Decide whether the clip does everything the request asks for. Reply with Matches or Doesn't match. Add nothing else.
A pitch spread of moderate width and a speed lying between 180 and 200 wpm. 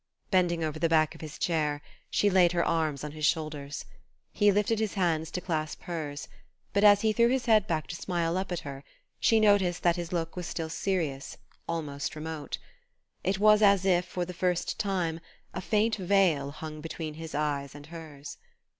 Matches